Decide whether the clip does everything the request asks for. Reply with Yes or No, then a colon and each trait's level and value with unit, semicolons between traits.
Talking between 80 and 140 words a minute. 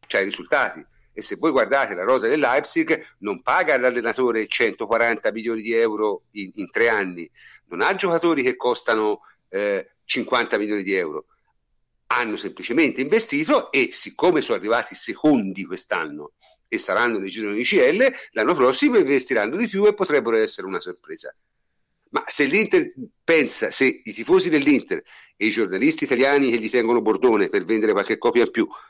No: average, 165 wpm